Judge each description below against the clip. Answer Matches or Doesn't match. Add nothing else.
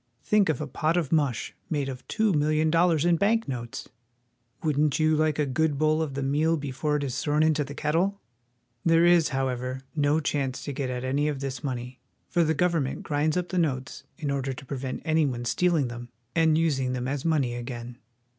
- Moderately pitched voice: Matches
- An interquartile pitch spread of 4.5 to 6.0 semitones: Doesn't match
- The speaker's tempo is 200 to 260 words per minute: Matches